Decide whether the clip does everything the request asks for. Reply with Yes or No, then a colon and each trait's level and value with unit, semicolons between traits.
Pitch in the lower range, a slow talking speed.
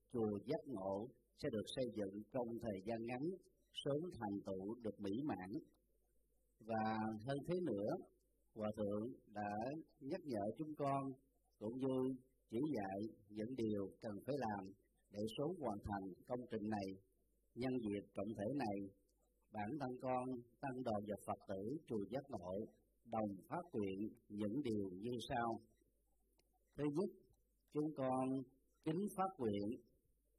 Yes: low, 115 Hz; slow, 145 wpm